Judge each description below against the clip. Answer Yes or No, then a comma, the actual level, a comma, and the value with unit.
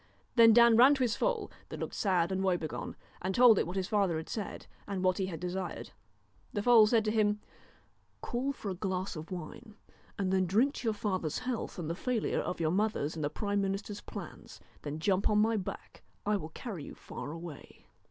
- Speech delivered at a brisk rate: Yes, fast, 210 wpm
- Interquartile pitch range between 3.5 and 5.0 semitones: Yes, average, 3.8 semitones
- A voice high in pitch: Yes, high, 195 Hz